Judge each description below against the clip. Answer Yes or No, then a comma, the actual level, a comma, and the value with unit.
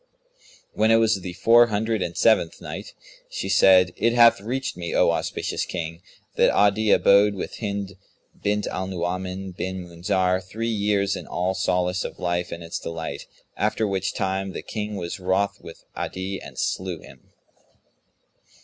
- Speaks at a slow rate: No, average, 160 wpm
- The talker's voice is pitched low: Yes, very low, 95 Hz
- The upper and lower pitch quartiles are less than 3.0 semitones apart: Yes, narrow, 2.5 semitones